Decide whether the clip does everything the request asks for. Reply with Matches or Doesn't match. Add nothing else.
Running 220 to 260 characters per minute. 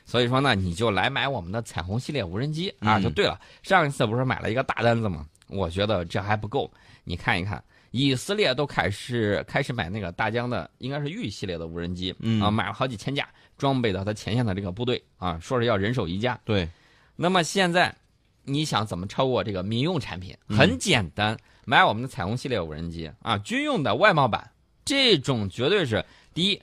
Doesn't match